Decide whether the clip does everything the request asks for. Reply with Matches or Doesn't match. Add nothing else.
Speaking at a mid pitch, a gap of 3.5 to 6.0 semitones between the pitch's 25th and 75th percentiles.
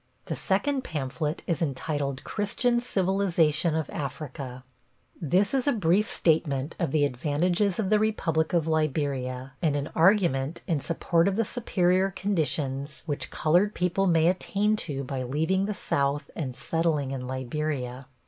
Matches